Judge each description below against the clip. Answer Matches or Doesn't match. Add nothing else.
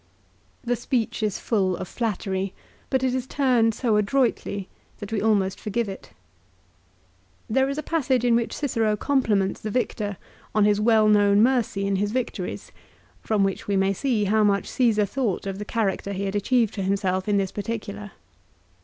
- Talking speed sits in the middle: Matches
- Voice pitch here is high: Matches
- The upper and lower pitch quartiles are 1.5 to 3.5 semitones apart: Matches